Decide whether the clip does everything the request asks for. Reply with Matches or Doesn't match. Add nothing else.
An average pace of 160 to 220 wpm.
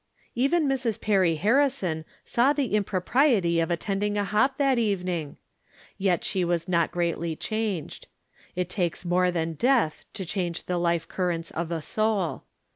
Doesn't match